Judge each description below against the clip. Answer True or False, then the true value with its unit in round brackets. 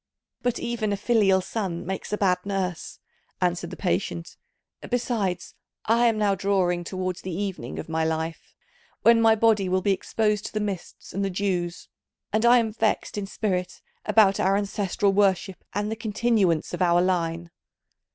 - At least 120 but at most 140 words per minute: False (170 wpm)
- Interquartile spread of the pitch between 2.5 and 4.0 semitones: True (2.9 semitones)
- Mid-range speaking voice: False (195 Hz)